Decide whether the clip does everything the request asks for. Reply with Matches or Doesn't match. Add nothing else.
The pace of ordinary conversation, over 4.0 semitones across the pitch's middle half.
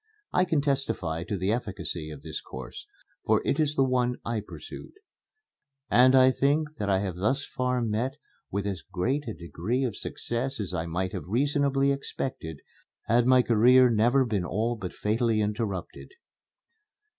Matches